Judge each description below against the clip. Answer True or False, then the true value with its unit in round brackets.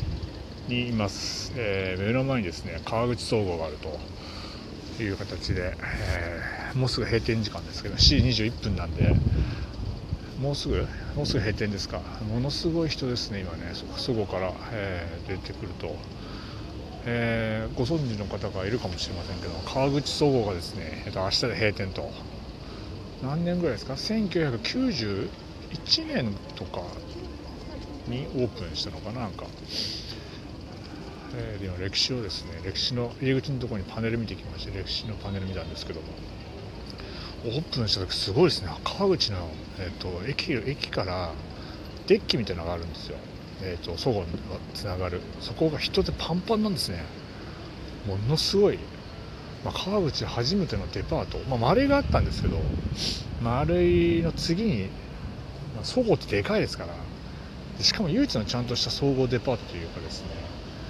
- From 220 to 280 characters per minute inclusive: False (310 characters per minute)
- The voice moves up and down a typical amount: True (5.0 semitones)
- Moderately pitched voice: False (105 Hz)